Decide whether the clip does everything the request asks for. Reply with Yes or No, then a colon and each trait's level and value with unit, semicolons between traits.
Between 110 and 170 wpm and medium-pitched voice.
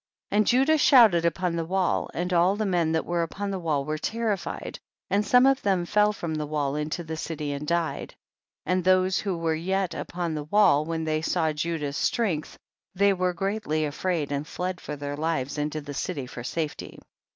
No: average, 200 wpm; medium, 170 Hz